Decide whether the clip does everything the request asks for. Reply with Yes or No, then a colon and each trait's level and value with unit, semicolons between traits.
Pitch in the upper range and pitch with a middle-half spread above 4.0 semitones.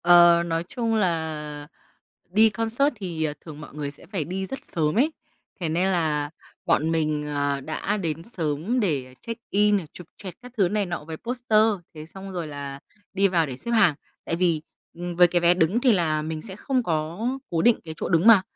No: medium, 170 Hz; average, 4.8 semitones